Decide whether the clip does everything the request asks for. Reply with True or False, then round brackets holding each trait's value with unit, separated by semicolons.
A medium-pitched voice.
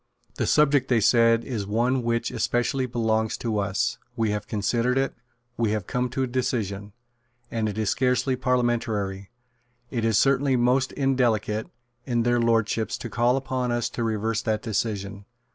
False (115 Hz)